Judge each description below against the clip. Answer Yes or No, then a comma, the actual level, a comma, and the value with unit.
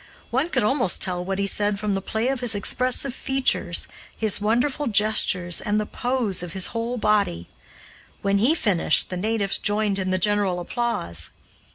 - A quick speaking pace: No, average, 175 wpm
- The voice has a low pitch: No, high, 210 Hz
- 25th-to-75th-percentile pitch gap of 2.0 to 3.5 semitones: No, average, 3.9 semitones